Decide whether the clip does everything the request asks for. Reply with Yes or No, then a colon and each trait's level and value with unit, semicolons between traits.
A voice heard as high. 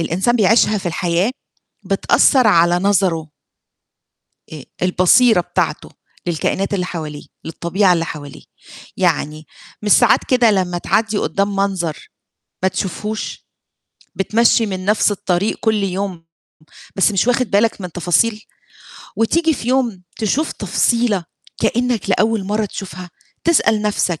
Yes: high, 195 Hz